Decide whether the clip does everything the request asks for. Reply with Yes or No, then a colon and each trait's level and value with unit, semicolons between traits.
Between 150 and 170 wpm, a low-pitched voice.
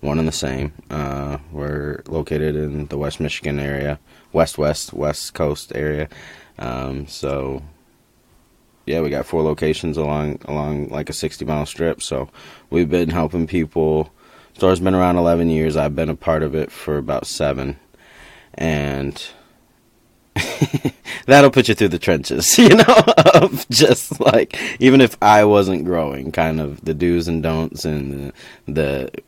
Yes: average, 155 wpm; very low, 75 Hz